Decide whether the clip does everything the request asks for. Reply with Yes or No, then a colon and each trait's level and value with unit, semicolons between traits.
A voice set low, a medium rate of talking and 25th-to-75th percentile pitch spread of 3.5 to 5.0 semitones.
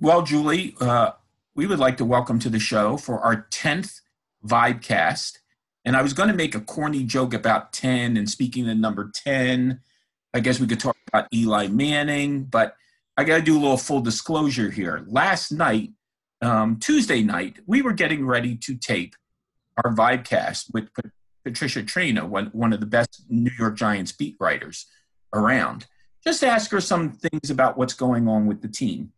Yes: low, 125 Hz; average, 180 wpm; average, 4.6 semitones